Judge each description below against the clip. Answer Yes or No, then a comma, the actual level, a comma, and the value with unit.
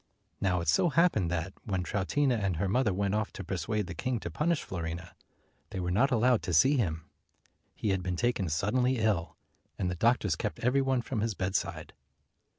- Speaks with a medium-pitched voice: No, low, 100 Hz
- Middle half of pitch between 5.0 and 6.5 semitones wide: Yes, wide, 5.6 semitones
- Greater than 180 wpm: Yes, average, 195 wpm